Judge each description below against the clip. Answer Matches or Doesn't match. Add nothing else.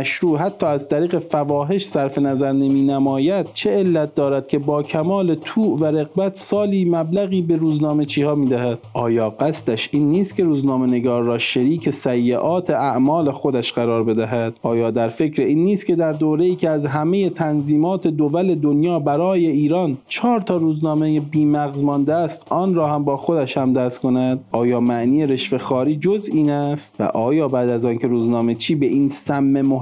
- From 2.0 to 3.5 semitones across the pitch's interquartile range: Doesn't match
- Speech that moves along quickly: Matches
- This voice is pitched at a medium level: Matches